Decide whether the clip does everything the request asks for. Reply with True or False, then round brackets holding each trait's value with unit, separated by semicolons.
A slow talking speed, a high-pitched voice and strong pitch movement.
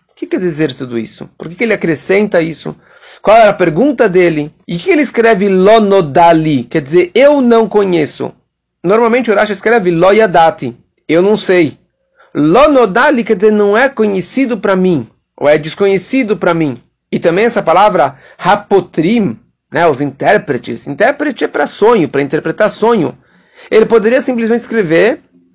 False (160 wpm; 195 Hz; 5.8 semitones)